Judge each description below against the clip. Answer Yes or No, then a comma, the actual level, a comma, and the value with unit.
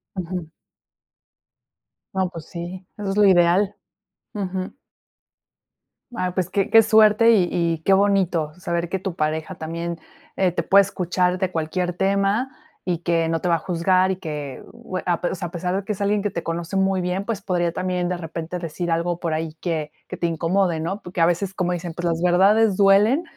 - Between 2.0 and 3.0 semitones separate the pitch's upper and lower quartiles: Yes, narrow, 2.4 semitones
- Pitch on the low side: No, medium, 180 Hz